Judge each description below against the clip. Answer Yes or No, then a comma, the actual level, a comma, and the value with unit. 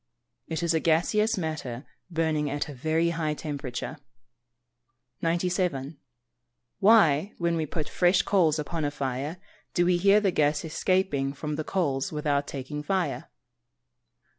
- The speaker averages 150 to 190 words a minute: No, average, 140 wpm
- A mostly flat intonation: No, average, 3.3 semitones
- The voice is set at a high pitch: No, medium, 160 Hz